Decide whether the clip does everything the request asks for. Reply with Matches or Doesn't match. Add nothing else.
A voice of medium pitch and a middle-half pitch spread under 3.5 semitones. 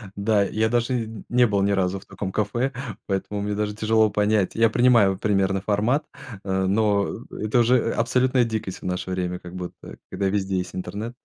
Doesn't match